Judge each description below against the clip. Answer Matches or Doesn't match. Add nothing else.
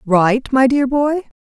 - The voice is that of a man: Doesn't match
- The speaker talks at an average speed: Matches